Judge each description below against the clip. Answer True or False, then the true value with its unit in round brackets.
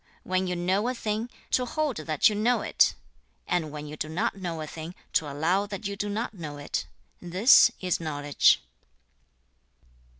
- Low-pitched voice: False (180 Hz)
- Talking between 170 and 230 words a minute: True (175 wpm)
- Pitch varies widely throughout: False (5.0 semitones)